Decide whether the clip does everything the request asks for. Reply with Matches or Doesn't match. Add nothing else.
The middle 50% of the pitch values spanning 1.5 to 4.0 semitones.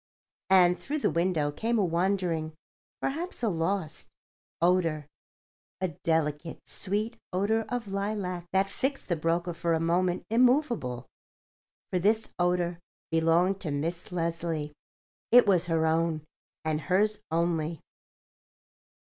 Matches